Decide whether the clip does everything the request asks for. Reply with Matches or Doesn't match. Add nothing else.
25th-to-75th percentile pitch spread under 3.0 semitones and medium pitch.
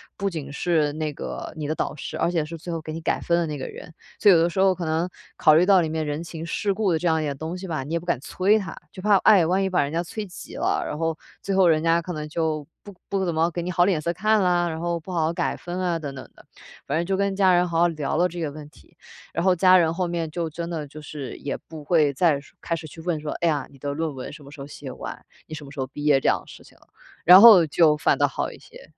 Matches